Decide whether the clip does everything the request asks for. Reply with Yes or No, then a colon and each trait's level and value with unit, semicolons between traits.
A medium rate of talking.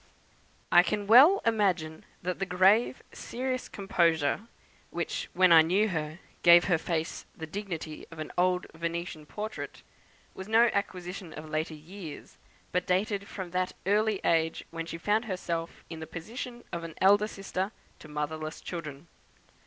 Yes: average, 155 wpm